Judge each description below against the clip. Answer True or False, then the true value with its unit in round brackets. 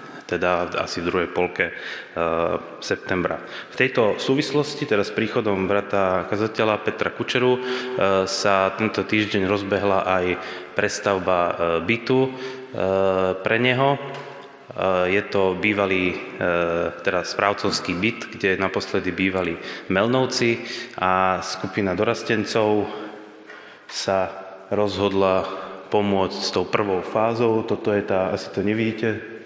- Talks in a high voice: False (100 Hz)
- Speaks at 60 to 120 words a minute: True (115 wpm)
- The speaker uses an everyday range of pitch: True (3.2 semitones)